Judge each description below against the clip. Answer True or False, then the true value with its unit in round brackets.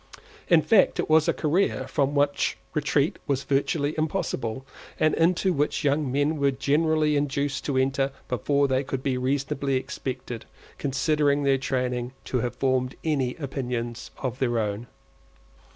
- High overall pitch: False (140 Hz)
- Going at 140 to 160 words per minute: True (150 wpm)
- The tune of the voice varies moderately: False (2.3 semitones)